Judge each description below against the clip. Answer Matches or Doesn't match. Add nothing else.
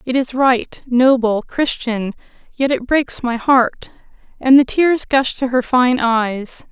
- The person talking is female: Matches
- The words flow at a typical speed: Matches